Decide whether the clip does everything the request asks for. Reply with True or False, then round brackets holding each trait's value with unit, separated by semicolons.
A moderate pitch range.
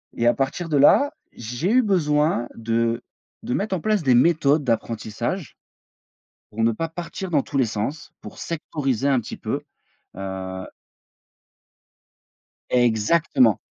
False (6.1 semitones)